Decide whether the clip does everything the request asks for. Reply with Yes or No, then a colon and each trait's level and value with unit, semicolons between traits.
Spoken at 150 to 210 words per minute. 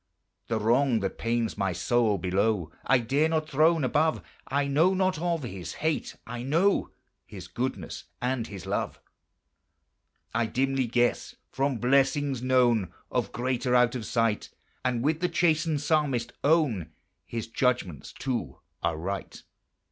No: average, 140 wpm